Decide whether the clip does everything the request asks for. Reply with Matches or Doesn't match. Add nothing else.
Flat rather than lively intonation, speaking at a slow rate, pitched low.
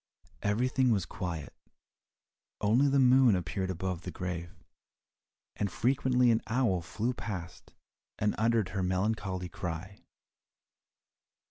Doesn't match